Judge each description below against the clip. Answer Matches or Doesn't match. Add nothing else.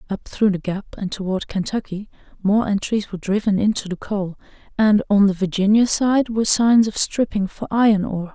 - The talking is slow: Doesn't match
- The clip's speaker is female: Matches